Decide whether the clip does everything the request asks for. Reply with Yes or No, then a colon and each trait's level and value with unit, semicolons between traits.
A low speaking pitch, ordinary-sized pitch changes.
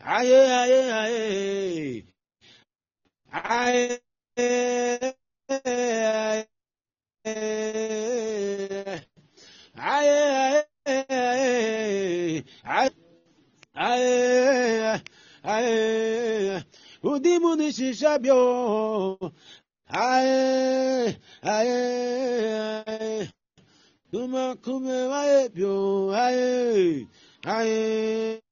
No: high, 240 Hz; average, 3.1 semitones